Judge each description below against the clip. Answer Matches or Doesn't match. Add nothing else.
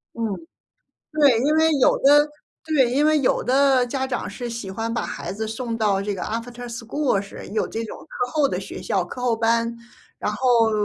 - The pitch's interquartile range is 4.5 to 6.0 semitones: Doesn't match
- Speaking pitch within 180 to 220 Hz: Doesn't match